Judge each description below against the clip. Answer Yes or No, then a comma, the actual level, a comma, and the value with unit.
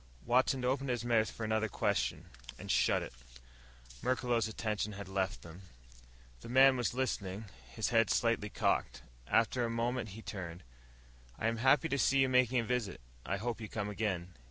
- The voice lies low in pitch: Yes, low, 115 Hz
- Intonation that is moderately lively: Yes, average, 3.3 semitones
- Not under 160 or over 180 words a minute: Yes, average, 175 wpm